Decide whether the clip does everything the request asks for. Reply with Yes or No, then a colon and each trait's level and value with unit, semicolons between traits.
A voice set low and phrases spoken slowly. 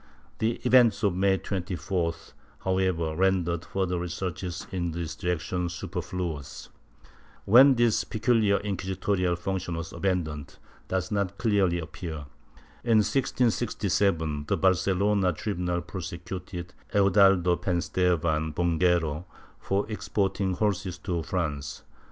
Yes: very low, 90 Hz; slow, 105 wpm